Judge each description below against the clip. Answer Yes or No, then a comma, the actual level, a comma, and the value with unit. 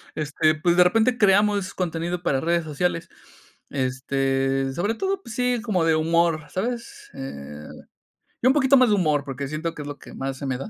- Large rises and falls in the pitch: Yes, wide, 6.8 semitones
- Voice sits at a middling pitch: Yes, medium, 165 Hz